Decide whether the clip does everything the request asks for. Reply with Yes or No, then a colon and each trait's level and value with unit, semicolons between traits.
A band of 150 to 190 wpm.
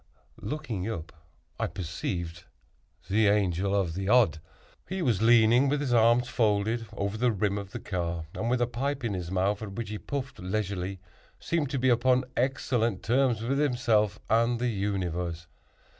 Yes: average, 170 wpm